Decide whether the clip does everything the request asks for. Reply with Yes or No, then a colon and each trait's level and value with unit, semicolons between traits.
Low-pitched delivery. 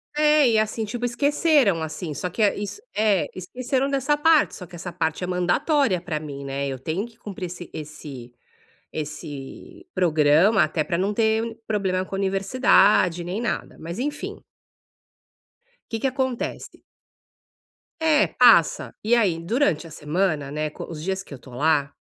No: high, 190 Hz